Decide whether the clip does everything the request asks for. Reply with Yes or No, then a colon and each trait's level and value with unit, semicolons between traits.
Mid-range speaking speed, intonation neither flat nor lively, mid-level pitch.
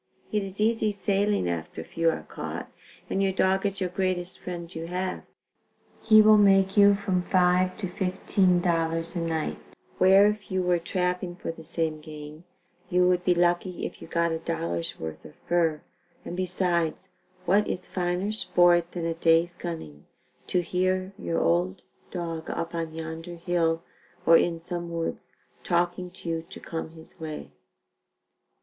No: average, 165 wpm; narrow, 2.2 semitones; medium, 175 Hz